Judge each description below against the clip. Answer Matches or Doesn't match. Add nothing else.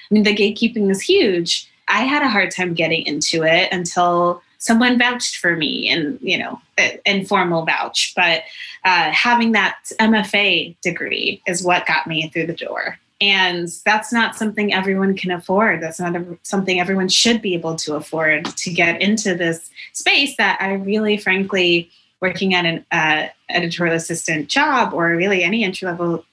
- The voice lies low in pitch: Doesn't match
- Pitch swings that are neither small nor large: Matches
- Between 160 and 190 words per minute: Matches